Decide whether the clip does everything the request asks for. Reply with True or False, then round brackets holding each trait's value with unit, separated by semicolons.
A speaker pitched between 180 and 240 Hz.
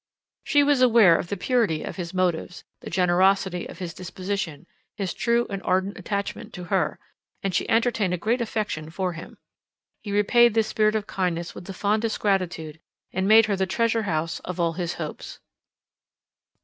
True (190 Hz)